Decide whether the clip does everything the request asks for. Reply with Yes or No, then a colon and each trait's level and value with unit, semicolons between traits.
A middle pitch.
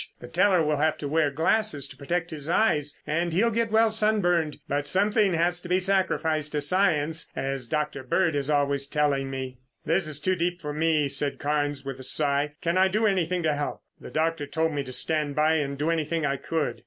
Yes: medium, 155 Hz